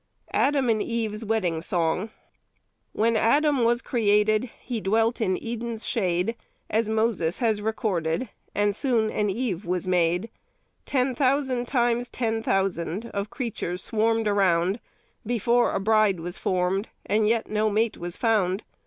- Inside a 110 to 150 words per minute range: Yes, average, 140 wpm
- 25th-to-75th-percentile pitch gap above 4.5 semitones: No, average, 3.4 semitones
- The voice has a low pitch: No, high, 220 Hz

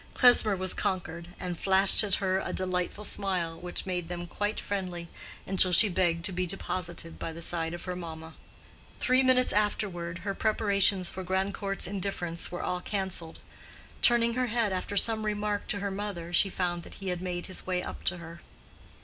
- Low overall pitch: No, medium, 185 Hz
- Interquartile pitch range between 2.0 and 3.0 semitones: Yes, narrow, 2.6 semitones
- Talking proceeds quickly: No, average, 185 wpm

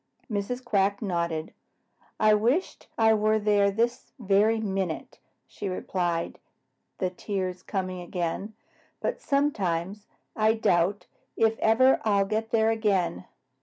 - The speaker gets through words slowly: Yes, slow, 120 wpm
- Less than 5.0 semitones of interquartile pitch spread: Yes, average, 3.2 semitones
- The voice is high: Yes, high, 205 Hz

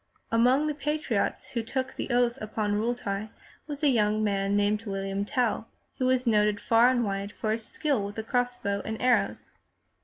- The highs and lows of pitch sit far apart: No, average, 3.3 semitones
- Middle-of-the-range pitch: No, high, 225 Hz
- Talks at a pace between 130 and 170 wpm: No, average, 185 wpm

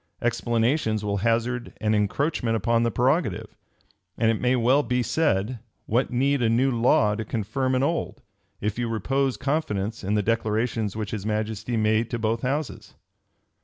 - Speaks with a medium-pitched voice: No, low, 115 Hz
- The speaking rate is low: No, average, 165 wpm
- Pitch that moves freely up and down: No, average, 2.7 semitones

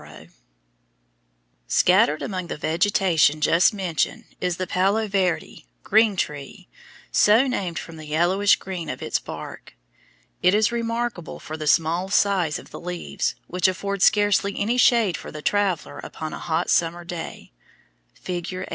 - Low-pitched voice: No, medium, 180 Hz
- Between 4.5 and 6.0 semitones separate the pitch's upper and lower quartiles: No, average, 3.6 semitones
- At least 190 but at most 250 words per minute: No, average, 150 wpm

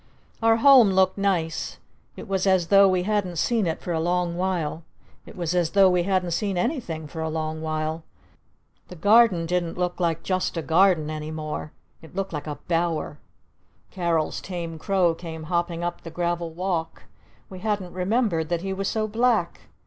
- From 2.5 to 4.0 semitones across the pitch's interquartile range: Yes, average, 2.9 semitones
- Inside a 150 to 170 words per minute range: No, average, 180 wpm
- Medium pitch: Yes, medium, 175 Hz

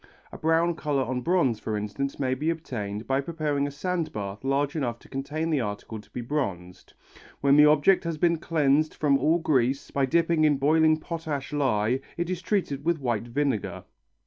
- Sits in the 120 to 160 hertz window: Yes, medium, 140 Hz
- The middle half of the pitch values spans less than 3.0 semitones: No, average, 4.0 semitones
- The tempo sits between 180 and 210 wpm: Yes, average, 190 wpm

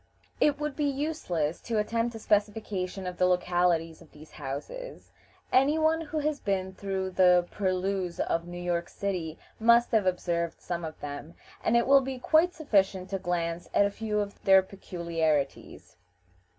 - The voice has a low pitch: No, high, 190 Hz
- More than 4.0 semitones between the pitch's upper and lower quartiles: Yes, average, 5.1 semitones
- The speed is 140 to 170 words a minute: Yes, average, 165 wpm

